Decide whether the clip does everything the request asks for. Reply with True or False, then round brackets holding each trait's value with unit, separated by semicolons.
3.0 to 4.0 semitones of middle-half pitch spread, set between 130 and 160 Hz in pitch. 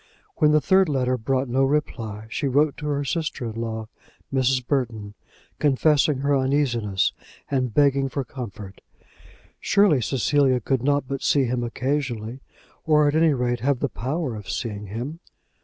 True (3.4 semitones; 135 Hz)